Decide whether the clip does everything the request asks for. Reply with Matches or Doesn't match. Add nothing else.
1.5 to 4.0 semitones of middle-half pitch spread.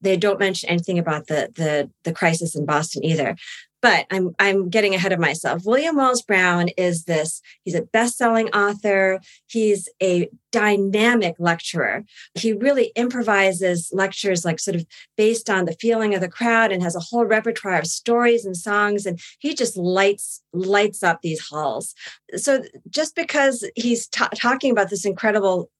Doesn't match